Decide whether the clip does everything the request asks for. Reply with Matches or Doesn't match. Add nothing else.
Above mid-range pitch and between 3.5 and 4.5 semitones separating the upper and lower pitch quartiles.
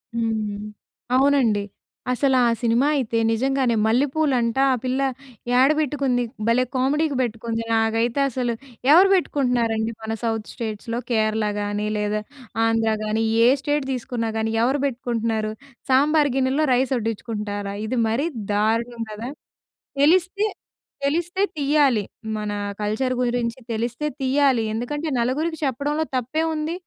Matches